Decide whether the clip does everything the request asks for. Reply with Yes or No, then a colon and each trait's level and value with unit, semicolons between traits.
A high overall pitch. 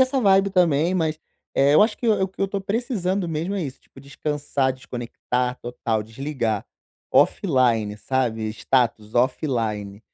No: medium, 140 Hz